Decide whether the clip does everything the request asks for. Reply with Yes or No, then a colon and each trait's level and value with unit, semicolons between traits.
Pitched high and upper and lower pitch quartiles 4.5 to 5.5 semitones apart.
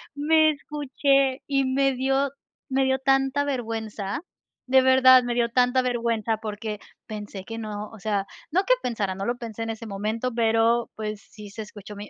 No: high, 235 Hz; average, 3.6 semitones